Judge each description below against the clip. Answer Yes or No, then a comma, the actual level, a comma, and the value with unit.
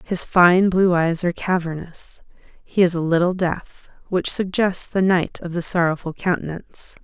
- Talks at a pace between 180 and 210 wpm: No, average, 160 wpm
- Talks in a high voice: No, medium, 175 Hz